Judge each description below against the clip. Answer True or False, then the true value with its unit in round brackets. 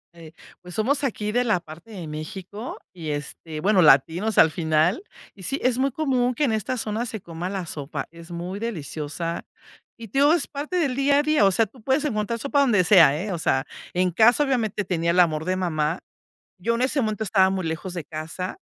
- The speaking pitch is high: True (195 Hz)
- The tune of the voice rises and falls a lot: True (6.5 semitones)